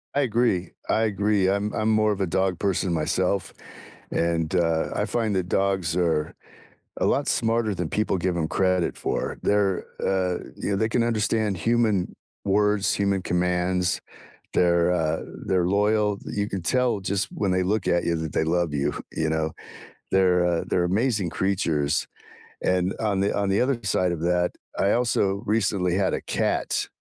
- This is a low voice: Yes, very low, 95 Hz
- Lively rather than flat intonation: No, average, 2.9 semitones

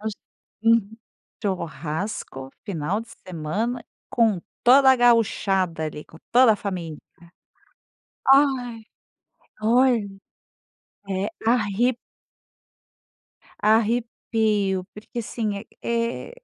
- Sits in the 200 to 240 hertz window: Yes, high, 215 Hz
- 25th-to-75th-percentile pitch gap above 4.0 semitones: No, average, 3.7 semitones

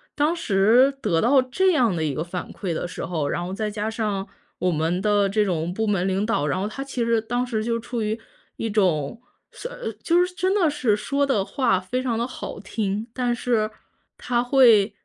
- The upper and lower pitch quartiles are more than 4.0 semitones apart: Yes, average, 4.6 semitones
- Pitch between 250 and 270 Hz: No, high, 220 Hz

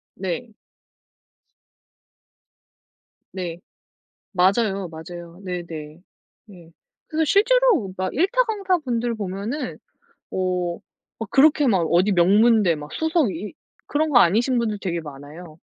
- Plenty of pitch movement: Yes, wide, 6.7 semitones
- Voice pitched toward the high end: Yes, high, 195 Hz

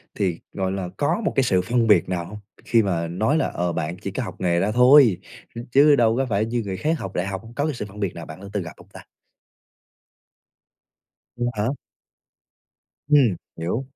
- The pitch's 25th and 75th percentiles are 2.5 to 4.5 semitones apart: No, average, 5.1 semitones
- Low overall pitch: Yes, low, 105 Hz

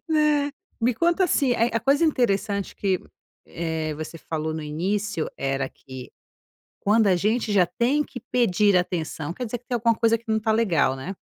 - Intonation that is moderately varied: No, wide, 6.6 semitones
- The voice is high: Yes, high, 210 Hz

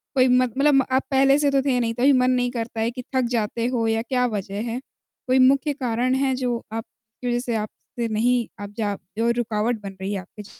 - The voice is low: No, high, 240 Hz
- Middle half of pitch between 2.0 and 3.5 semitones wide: Yes, narrow, 2.5 semitones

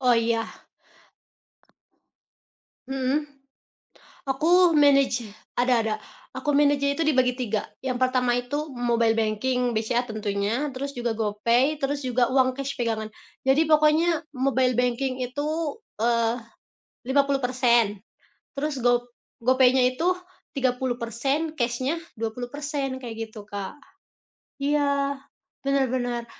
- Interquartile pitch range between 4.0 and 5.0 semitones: No, average, 2.9 semitones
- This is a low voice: No, very high, 255 Hz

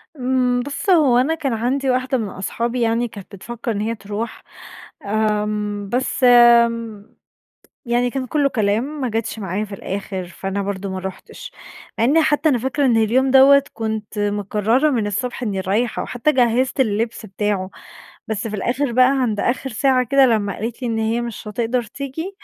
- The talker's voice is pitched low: No, high, 235 Hz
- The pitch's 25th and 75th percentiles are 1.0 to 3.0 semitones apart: No, average, 3.7 semitones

